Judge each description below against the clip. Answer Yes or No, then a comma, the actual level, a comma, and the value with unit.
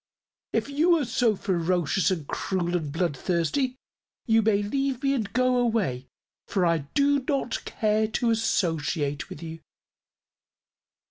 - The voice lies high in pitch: Yes, high, 205 Hz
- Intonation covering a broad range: Yes, wide, 6.9 semitones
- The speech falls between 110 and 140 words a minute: Yes, slow, 135 wpm